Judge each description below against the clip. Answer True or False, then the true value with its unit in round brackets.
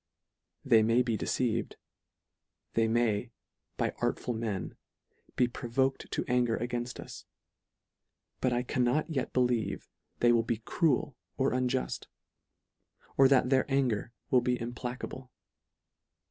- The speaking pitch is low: True (125 Hz)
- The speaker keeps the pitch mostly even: True (1.8 semitones)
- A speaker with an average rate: False (125 wpm)